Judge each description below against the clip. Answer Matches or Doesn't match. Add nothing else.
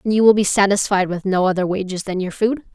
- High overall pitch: Matches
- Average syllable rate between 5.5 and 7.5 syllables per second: Matches